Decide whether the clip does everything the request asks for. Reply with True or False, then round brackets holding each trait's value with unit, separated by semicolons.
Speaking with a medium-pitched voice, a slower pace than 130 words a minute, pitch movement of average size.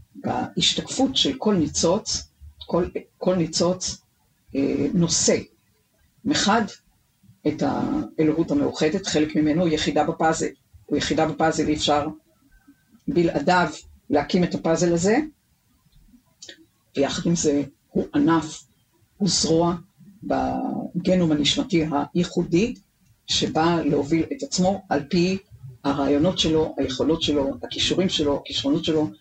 True (160 Hz; 105 wpm; 3.5 semitones)